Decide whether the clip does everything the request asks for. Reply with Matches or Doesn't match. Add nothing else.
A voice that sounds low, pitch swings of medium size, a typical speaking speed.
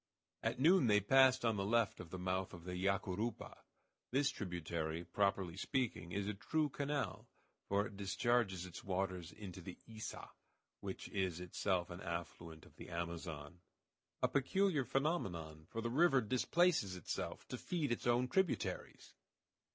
Doesn't match